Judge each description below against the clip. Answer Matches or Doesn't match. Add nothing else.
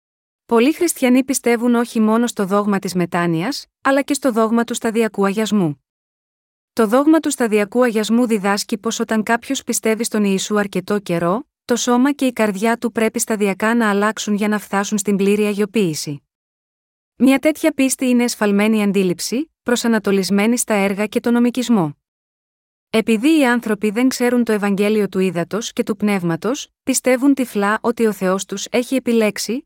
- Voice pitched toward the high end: Matches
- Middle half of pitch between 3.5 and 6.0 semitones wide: Doesn't match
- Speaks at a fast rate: Doesn't match